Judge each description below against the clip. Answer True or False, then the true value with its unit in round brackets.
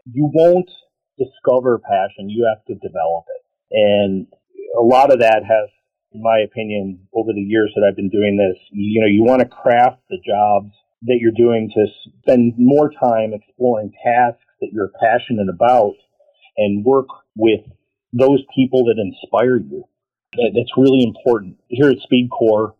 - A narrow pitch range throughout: False (3.8 semitones)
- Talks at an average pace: True (160 wpm)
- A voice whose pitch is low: True (115 Hz)